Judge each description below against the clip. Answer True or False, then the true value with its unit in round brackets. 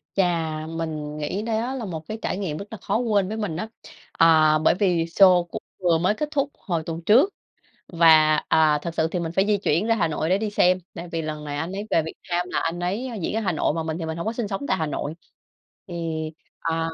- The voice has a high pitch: False (175 Hz)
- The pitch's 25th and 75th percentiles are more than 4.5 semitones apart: False (4.2 semitones)